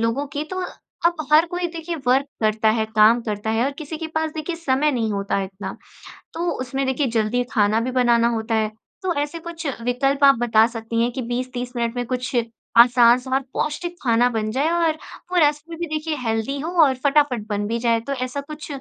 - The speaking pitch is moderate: No, very high, 255 Hz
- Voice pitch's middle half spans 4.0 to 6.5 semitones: Yes, average, 4.8 semitones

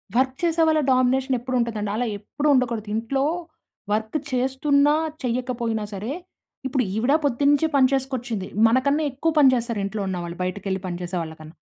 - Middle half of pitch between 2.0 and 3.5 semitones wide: No, average, 3.9 semitones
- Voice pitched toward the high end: Yes, very high, 250 Hz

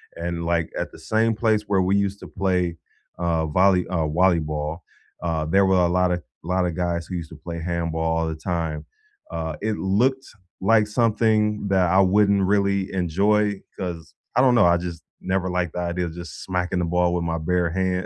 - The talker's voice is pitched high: No, very low, 90 Hz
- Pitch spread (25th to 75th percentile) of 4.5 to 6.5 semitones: No, average, 2.8 semitones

